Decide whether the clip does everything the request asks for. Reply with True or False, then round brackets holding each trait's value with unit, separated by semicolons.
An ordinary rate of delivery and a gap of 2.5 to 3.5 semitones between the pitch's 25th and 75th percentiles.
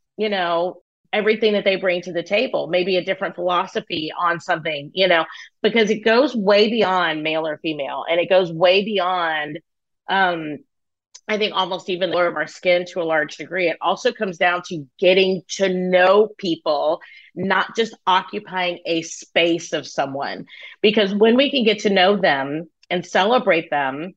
True (175 wpm; 3.2 semitones)